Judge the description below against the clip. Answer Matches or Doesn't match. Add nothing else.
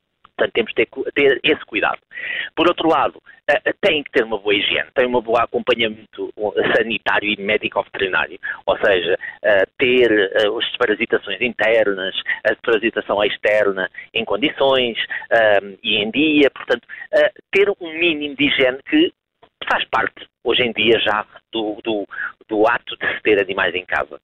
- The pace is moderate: Matches